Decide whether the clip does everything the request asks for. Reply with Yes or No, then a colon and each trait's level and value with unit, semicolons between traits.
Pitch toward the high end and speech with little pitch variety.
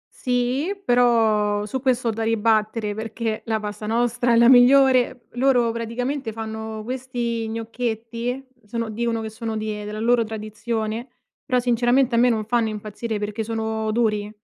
Yes: high, 230 Hz; narrow, 2.0 semitones